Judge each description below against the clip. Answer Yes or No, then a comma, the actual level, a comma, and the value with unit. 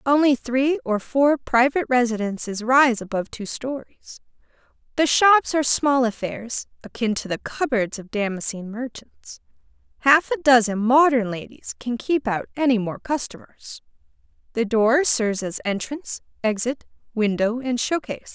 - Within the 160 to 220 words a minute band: No, slow, 135 wpm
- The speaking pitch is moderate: No, high, 245 Hz